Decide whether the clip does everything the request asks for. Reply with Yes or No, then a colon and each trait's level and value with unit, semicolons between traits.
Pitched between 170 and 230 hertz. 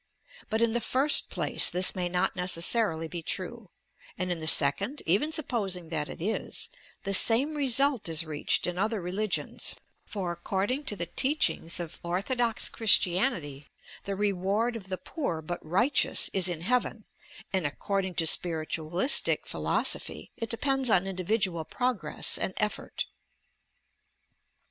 Yes: high, 190 Hz